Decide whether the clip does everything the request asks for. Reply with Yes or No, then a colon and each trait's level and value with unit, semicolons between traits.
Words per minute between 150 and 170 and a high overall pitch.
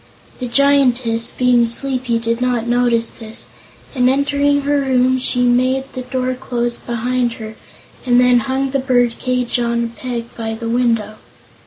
Yes: average, 160 wpm; high, 245 Hz